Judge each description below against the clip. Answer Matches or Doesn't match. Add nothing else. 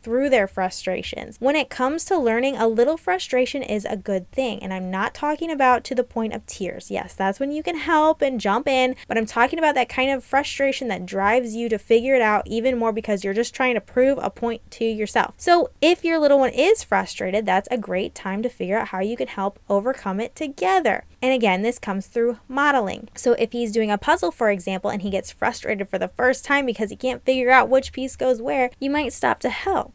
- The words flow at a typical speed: Doesn't match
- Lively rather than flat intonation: Doesn't match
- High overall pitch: Matches